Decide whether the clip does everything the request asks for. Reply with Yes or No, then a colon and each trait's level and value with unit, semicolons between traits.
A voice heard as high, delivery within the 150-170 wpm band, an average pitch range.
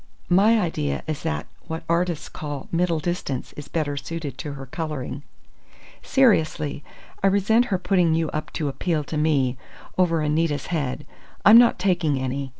No: medium, 160 Hz; average, 155 wpm; average, 3.8 semitones